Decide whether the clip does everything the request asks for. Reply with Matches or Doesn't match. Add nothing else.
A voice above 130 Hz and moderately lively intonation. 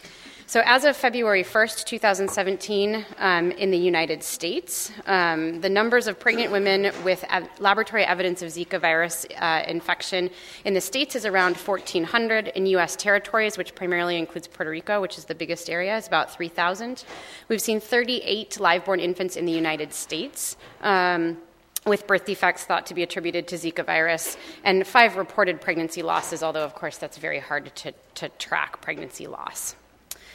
Matches